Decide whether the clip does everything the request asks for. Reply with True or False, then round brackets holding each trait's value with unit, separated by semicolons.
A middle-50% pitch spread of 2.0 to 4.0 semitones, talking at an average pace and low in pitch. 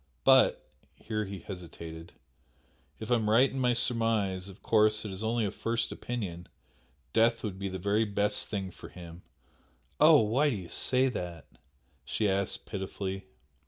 True (3.3 semitones; 160 wpm; 105 Hz)